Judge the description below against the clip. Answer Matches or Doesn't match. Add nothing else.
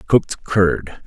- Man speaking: Matches